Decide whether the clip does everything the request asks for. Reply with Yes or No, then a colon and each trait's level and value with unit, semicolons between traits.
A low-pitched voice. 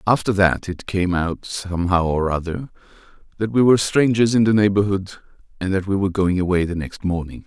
Yes: very low, 95 Hz